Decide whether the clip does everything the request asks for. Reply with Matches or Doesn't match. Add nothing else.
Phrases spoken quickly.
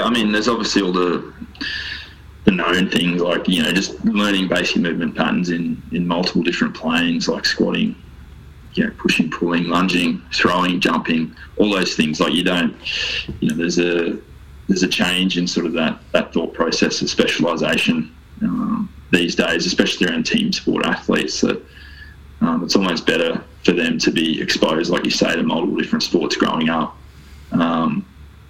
Doesn't match